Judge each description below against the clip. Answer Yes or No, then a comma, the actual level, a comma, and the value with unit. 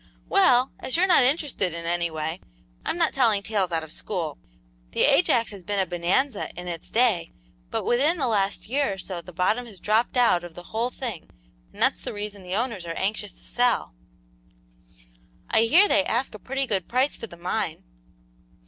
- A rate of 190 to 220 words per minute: Yes, average, 195 wpm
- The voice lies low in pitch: No, high, 210 Hz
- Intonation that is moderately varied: No, wide, 6.1 semitones